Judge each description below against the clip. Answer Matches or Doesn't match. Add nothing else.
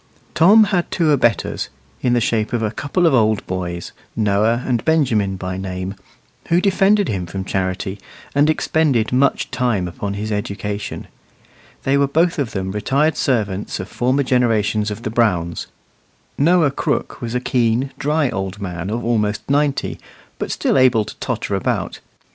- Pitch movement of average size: Doesn't match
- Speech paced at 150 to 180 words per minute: Matches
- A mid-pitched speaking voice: Doesn't match